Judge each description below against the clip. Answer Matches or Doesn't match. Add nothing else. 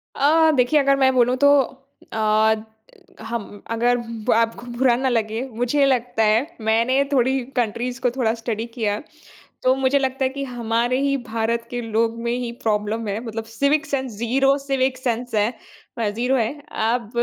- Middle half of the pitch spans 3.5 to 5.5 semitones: Doesn't match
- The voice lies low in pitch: Doesn't match